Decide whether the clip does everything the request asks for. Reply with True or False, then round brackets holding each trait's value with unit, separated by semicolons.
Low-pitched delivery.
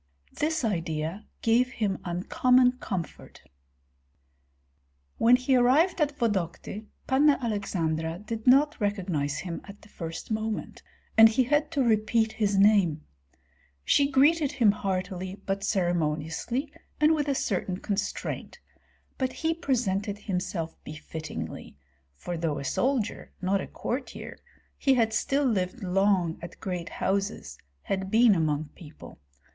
False (205 Hz)